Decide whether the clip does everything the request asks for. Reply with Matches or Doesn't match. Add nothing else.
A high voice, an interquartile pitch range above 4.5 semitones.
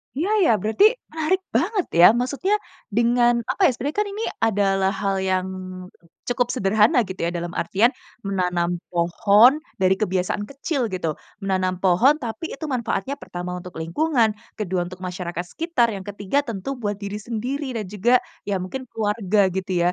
Matches